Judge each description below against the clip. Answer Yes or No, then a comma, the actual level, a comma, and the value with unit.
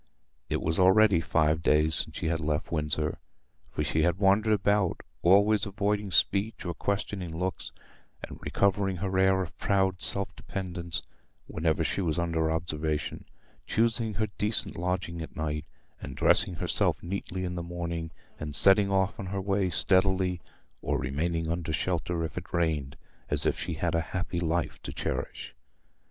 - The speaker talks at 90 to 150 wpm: No, average, 160 wpm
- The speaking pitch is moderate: No, very low, 90 Hz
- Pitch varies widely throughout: No, average, 3.2 semitones